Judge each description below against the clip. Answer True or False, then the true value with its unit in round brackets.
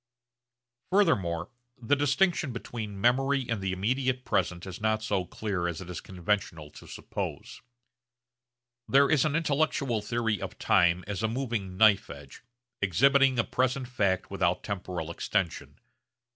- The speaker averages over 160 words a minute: False (140 wpm)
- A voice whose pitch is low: True (110 Hz)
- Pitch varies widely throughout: True (6.0 semitones)